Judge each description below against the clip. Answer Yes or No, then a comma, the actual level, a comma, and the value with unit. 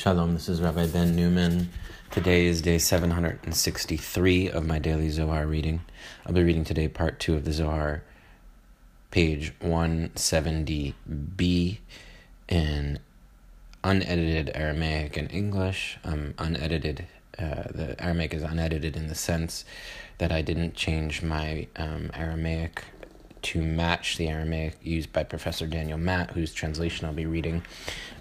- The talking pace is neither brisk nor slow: No, slow, 130 wpm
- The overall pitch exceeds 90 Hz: No, very low, 80 Hz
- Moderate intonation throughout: No, narrow, 1.6 semitones